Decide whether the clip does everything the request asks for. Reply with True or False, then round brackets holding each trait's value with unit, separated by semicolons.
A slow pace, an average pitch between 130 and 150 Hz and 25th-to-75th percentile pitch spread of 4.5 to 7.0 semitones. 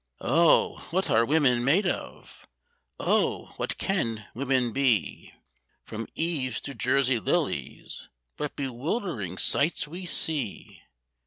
True (110 wpm; 135 Hz; 5.3 semitones)